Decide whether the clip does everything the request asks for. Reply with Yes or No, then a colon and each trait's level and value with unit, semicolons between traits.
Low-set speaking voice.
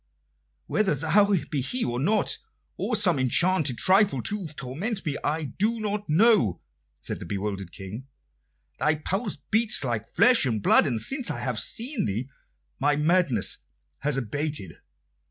No: medium, 150 Hz